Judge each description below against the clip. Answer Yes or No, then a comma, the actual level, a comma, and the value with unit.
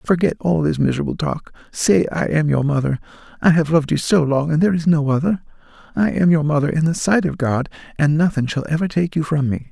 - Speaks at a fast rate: Yes, fast, 230 wpm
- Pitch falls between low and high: Yes, medium, 150 Hz